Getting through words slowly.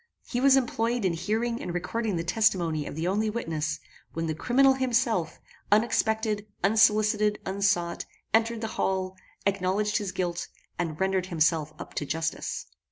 No: average, 150 wpm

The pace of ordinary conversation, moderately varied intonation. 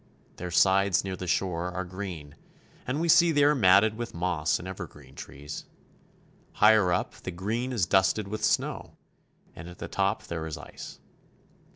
Yes: average, 170 wpm; average, 3.9 semitones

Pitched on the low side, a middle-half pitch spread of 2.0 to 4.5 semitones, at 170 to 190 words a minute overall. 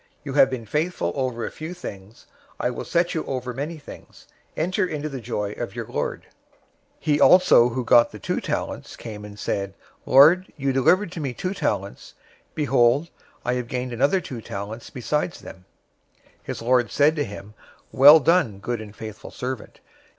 No: low, 130 Hz; average, 5.2 semitones; average, 180 wpm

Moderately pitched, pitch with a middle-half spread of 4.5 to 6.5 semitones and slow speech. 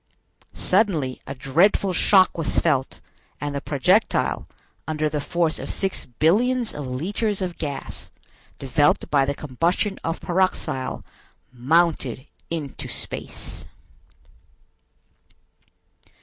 Yes: medium, 155 Hz; average, 5.2 semitones; slow, 105 wpm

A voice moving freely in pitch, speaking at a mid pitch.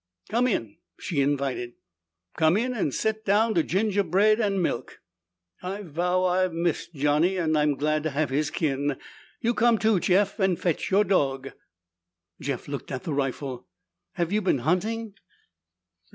Yes: wide, 5.8 semitones; medium, 175 Hz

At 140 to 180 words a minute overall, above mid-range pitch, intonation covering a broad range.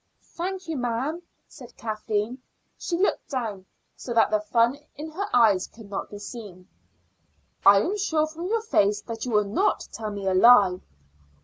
Yes: average, 175 wpm; high, 230 Hz; wide, 7.1 semitones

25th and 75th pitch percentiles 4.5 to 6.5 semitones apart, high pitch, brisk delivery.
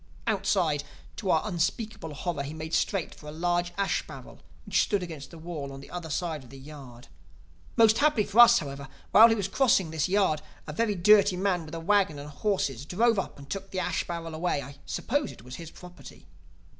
No: average, 4.9 semitones; medium, 175 Hz; fast, 210 wpm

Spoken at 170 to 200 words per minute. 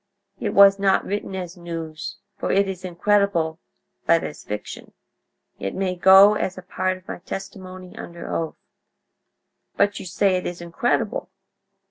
No: average, 150 wpm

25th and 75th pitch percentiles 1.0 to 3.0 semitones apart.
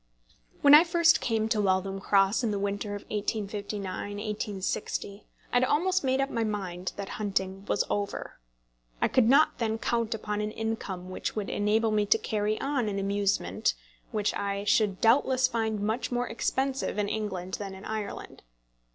Yes: narrow, 2.6 semitones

